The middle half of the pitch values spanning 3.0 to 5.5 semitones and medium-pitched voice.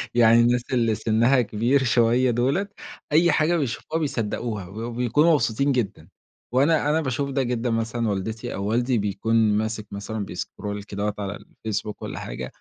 No: average, 3.5 semitones; low, 115 Hz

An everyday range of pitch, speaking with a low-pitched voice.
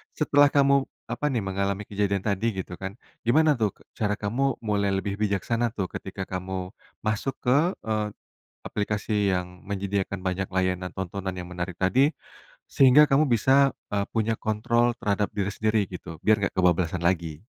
Yes: average, 3.8 semitones; low, 100 Hz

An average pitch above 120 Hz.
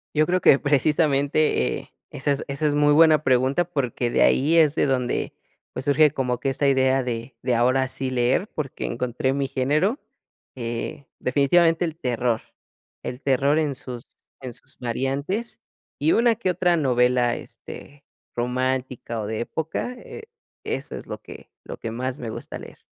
Yes: low, 135 Hz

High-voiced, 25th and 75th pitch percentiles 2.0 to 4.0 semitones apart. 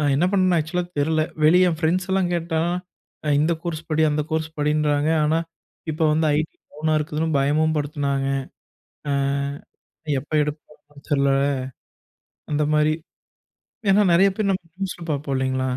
No: medium, 155 Hz; narrow, 2.5 semitones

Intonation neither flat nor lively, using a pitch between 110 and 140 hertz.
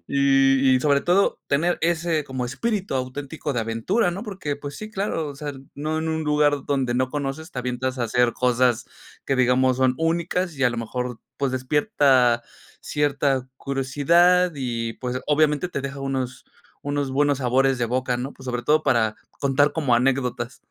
Yes: average, 3.0 semitones; low, 135 Hz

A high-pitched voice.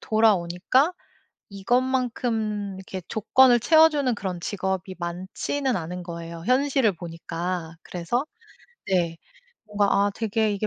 Yes: high, 205 Hz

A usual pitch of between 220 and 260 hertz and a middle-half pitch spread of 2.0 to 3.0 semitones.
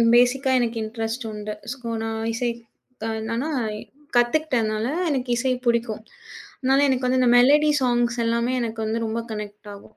Yes: high, 240 Hz; narrow, 2.4 semitones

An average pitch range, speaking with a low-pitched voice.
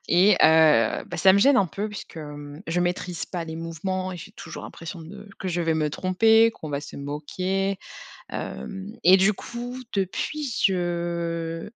No: average, 3.2 semitones; medium, 175 Hz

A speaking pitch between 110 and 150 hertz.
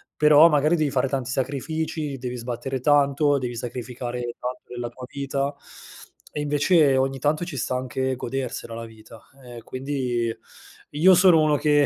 Yes: low, 135 Hz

